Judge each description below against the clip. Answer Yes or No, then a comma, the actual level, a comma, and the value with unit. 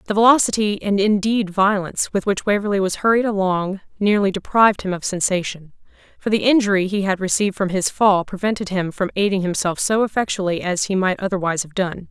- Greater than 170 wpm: Yes, average, 190 wpm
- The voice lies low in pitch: No, high, 195 Hz